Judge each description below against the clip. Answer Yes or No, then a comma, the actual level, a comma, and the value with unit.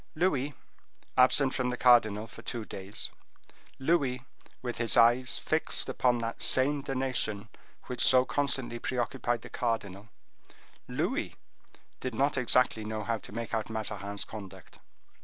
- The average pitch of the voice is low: Yes, low, 120 Hz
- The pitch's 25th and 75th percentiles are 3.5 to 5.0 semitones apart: No, average, 2.9 semitones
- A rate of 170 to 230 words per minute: No, slow, 135 wpm